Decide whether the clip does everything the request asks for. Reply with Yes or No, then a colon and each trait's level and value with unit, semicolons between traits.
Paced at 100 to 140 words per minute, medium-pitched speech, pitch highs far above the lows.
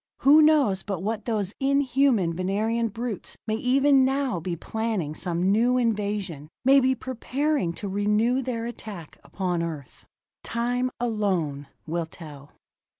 No: slow, 135 wpm; high, 220 Hz; wide, 5.7 semitones